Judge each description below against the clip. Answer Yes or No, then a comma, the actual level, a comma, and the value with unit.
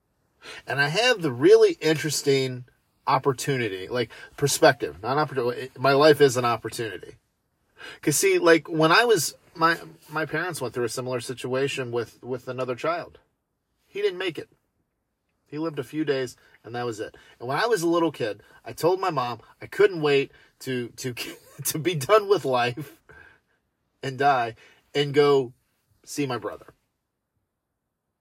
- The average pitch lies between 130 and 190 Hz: Yes, medium, 140 Hz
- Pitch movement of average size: Yes, average, 3.9 semitones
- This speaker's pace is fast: No, average, 160 wpm